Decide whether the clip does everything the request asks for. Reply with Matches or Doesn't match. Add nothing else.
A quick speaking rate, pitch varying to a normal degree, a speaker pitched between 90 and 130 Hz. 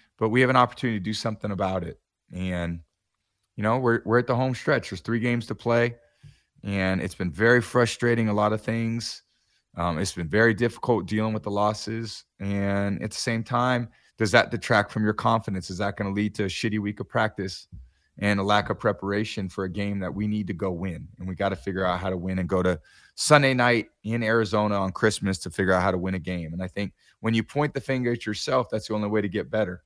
Matches